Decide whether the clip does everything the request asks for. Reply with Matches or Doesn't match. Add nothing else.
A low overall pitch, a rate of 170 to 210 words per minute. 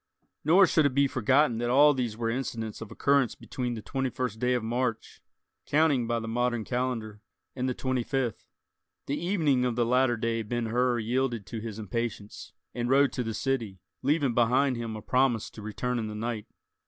Matches